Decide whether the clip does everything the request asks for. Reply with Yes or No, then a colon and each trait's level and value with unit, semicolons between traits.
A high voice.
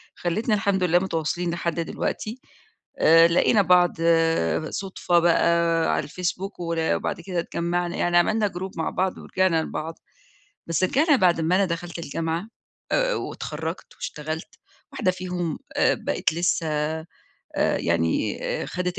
No: medium, 175 Hz